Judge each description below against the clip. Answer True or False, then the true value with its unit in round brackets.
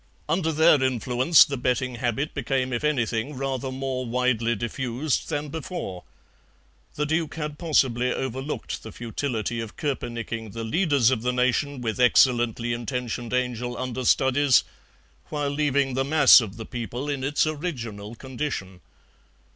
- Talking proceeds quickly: False (140 wpm)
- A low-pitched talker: True (130 Hz)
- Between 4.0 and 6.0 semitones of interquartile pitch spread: False (3.3 semitones)